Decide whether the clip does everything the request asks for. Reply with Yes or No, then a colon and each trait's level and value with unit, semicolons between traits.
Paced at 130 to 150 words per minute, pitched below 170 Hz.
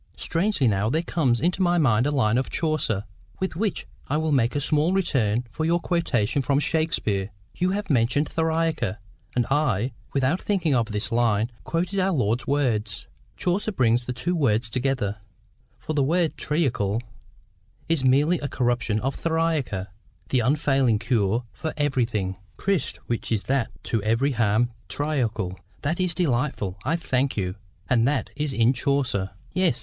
No: average, 160 wpm; low, 135 Hz